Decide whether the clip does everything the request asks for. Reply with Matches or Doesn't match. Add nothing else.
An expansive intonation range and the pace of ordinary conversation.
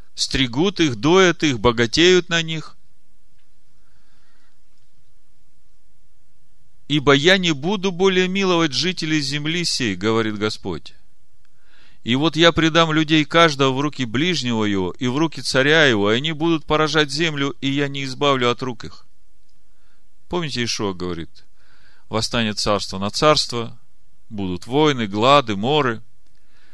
Matches